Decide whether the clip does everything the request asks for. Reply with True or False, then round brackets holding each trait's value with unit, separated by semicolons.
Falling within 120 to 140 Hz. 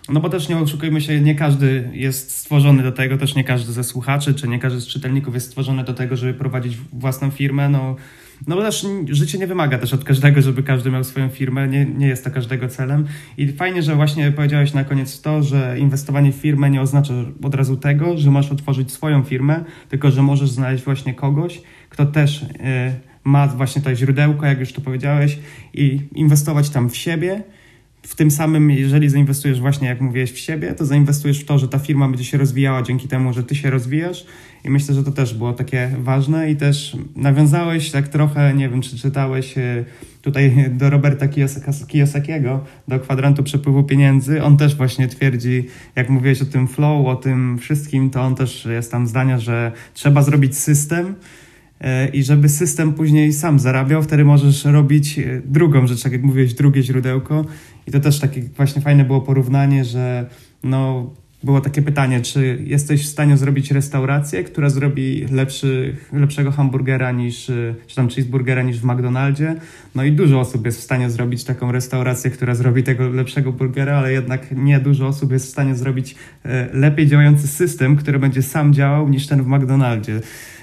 True (135 Hz)